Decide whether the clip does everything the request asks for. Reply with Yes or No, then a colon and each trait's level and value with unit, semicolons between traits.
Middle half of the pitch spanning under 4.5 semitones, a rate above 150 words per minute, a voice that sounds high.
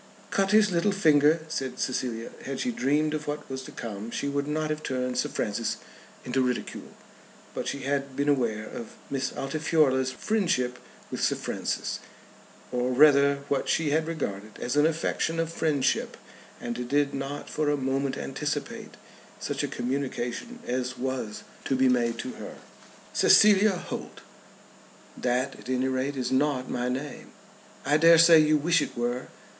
No: average, 3.4 semitones; average, 165 wpm; medium, 140 Hz